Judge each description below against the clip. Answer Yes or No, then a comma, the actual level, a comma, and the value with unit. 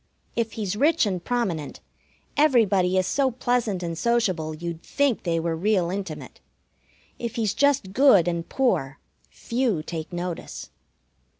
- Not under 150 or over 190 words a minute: No, slow, 135 wpm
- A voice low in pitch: No, high, 195 Hz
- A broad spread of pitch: Yes, wide, 5.9 semitones